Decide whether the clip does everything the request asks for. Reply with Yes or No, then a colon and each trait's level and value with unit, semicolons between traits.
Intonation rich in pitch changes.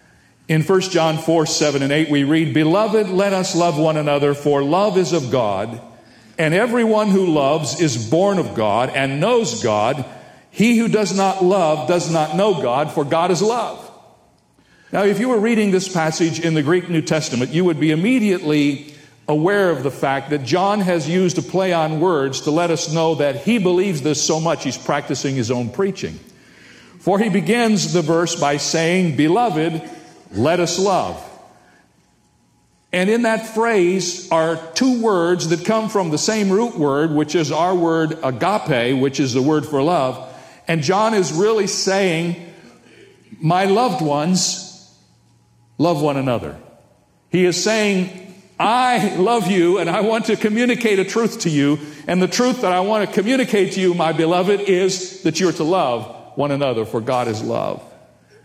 No: average, 4.5 semitones